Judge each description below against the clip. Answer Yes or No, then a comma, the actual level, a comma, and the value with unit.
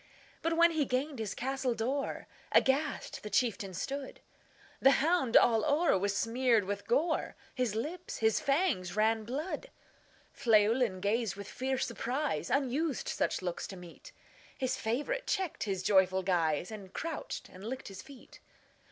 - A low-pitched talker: No, high, 240 Hz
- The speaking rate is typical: No, slow, 125 wpm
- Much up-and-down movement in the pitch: Yes, wide, 5.7 semitones